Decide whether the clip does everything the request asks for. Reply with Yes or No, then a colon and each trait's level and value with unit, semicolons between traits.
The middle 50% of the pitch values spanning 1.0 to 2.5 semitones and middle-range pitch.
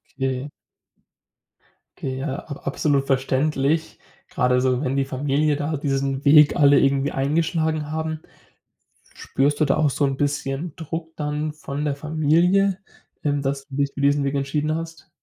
Yes: narrow, 2.1 semitones; medium, 145 Hz